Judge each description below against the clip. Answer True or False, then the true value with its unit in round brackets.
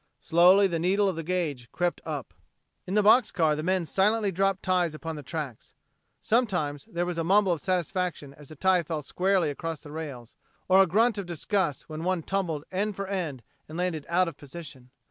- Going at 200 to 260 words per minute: True (205 wpm)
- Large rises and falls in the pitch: False (3.6 semitones)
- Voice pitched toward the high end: False (175 Hz)